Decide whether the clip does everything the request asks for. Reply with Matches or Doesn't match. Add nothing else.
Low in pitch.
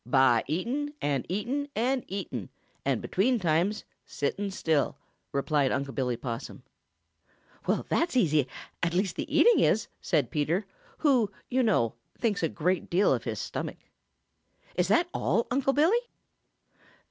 Doesn't match